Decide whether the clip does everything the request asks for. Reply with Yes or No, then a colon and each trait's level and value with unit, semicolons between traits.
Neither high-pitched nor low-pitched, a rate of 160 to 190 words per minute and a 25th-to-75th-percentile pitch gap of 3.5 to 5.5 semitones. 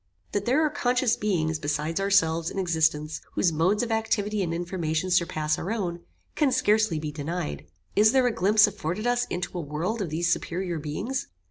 Yes: medium, 180 Hz; average, 185 wpm; average, 5.0 semitones